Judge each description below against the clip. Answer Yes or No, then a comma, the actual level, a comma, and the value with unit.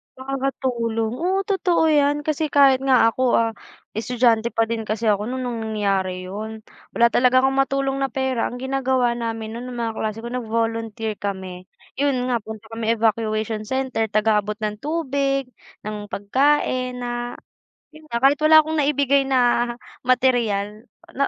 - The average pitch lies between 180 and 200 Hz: No, high, 240 Hz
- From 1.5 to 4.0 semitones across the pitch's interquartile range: Yes, average, 3.5 semitones